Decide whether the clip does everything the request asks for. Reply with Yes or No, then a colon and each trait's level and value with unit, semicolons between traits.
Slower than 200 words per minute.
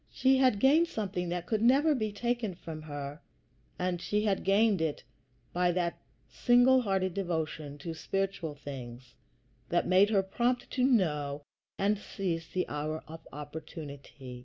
Yes: average, 150 wpm